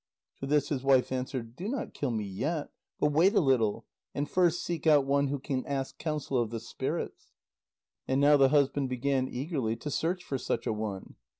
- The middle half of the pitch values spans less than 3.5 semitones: Yes, average, 2.8 semitones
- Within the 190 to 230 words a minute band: Yes, average, 200 wpm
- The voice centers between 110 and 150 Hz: Yes, medium, 140 Hz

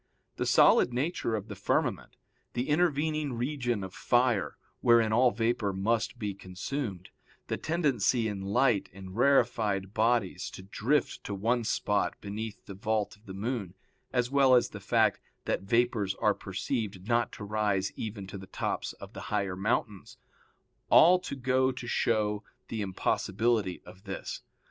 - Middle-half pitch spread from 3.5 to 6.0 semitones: Yes, average, 3.9 semitones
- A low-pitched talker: Yes, low, 110 Hz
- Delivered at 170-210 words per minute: No, average, 155 wpm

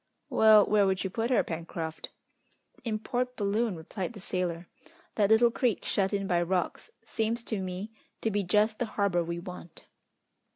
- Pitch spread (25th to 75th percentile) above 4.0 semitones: No, average, 3.5 semitones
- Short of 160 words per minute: No, average, 170 wpm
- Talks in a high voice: Yes, high, 200 Hz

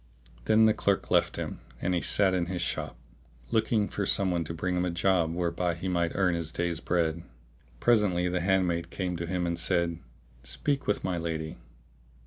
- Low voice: Yes, very low, 90 Hz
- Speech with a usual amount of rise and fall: No, narrow, 2.0 semitones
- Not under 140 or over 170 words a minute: No, average, 190 wpm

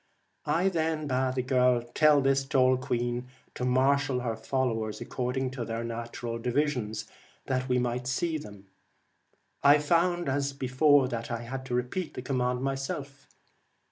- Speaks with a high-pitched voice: No, low, 130 Hz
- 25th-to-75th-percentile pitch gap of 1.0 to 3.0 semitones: Yes, narrow, 2.4 semitones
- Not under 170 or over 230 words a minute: No, average, 155 wpm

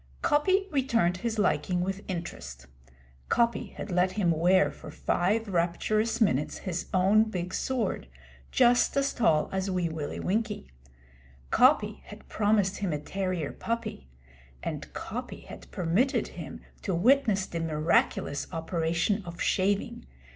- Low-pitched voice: No, high, 190 Hz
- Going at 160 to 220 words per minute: No, slow, 135 wpm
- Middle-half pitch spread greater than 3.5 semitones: Yes, average, 4.3 semitones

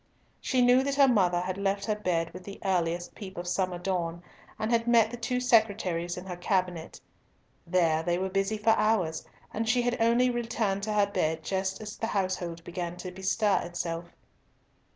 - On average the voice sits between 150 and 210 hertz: Yes, high, 190 Hz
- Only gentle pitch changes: No, average, 4.1 semitones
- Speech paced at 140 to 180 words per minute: No, average, 190 wpm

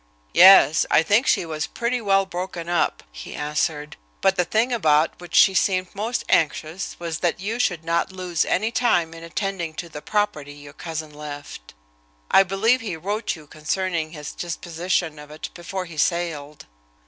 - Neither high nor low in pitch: Yes, medium, 170 Hz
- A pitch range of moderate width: Yes, average, 3.9 semitones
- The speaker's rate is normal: Yes, average, 170 wpm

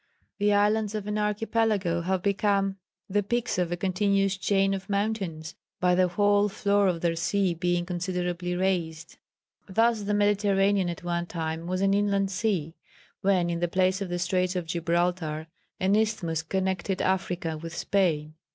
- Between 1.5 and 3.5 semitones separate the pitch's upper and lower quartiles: Yes, narrow, 2.6 semitones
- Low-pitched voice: No, high, 190 Hz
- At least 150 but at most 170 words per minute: Yes, average, 160 wpm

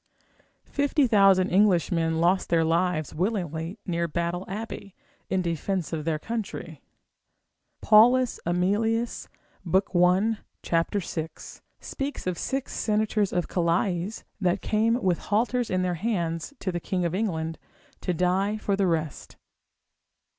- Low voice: No, medium, 185 Hz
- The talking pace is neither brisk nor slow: No, slow, 125 wpm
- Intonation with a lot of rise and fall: No, average, 3.9 semitones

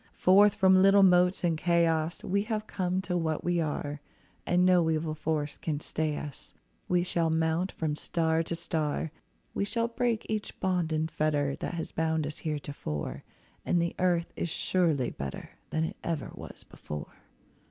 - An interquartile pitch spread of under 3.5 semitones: Yes, average, 2.7 semitones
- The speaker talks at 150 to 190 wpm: Yes, average, 170 wpm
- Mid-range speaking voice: Yes, medium, 165 Hz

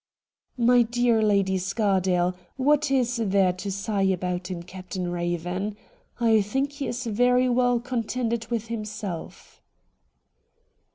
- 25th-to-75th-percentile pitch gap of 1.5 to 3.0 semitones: No, average, 4.5 semitones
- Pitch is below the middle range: No, high, 215 Hz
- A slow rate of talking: Yes, slow, 125 wpm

